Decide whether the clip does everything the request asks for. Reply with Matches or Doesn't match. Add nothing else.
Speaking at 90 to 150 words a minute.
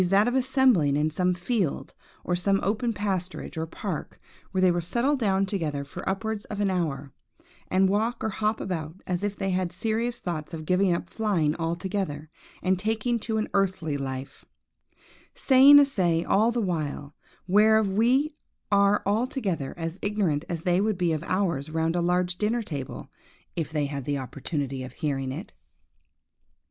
Doesn't match